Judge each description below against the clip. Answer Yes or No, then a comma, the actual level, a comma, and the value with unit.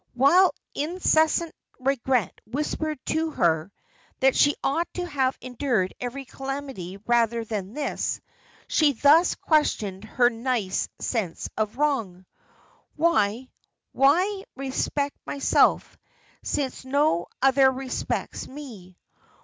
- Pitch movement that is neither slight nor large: Yes, average, 4.6 semitones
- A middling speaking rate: No, slow, 105 wpm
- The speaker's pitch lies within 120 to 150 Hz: No, very high, 265 Hz